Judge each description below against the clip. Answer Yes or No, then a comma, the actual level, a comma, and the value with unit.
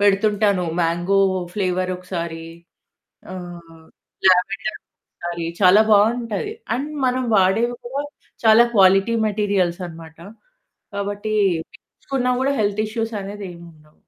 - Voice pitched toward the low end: No, high, 200 Hz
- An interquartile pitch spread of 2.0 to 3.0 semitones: No, average, 3.7 semitones